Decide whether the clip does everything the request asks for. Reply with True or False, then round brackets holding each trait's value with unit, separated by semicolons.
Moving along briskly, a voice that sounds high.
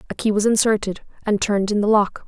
True (235 wpm; 210 Hz)